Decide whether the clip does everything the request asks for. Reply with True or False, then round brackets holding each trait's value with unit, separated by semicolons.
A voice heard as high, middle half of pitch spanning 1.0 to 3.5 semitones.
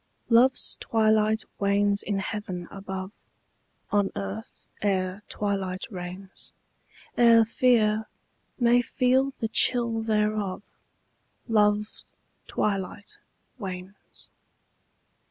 True (210 Hz; 2.7 semitones)